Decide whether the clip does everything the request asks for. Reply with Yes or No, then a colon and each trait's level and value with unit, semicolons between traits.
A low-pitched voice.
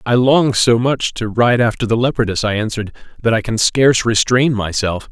Yes: low, 115 Hz